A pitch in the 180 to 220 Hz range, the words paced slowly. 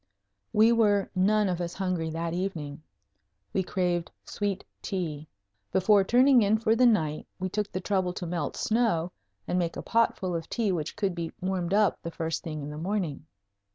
No: medium, 185 Hz; average, 185 wpm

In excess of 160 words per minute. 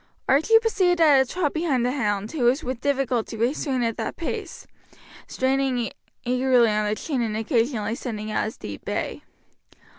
Yes: average, 170 wpm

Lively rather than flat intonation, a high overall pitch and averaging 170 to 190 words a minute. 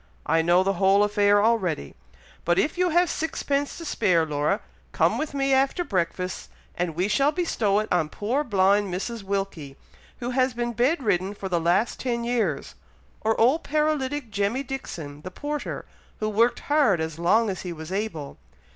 Yes: wide, 6.5 semitones; high, 205 Hz; average, 175 wpm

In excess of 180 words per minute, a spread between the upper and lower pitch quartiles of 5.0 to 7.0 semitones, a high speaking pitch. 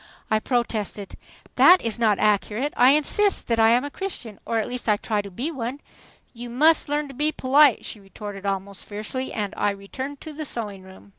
Yes: fast, 205 wpm; average, 5.3 semitones; high, 230 Hz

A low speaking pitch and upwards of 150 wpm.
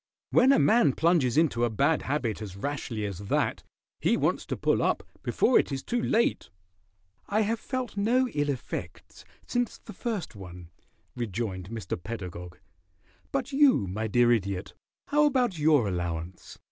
Yes: low, 130 Hz; average, 160 wpm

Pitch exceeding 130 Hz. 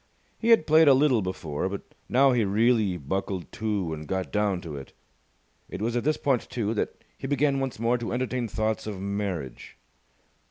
No: low, 110 Hz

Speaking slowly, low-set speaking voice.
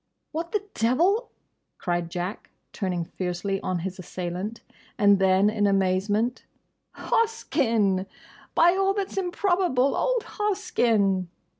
No: slow, 110 wpm; high, 215 Hz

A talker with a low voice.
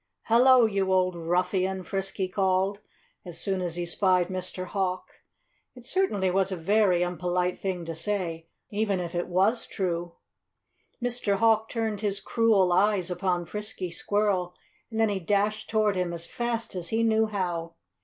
No: high, 190 Hz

